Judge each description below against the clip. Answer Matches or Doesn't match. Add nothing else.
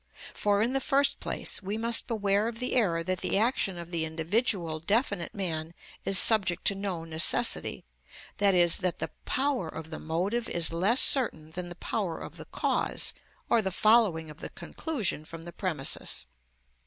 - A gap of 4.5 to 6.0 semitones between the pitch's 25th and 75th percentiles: Matches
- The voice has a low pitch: Doesn't match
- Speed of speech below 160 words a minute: Doesn't match